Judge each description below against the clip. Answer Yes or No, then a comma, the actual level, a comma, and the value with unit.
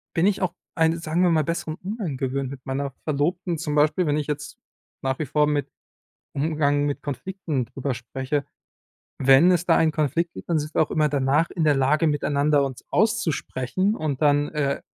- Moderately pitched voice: Yes, medium, 150 Hz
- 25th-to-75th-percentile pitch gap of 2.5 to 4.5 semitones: Yes, average, 2.9 semitones